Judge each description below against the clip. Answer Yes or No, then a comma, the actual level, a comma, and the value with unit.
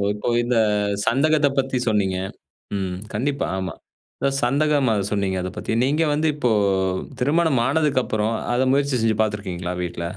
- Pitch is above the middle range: No, low, 120 Hz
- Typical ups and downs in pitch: No, wide, 6.0 semitones